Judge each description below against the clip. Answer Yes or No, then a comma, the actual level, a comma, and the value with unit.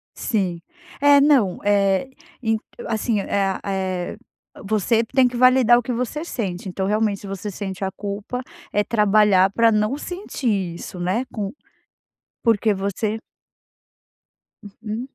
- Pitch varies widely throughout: No, average, 3.3 semitones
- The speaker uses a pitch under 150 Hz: No, high, 210 Hz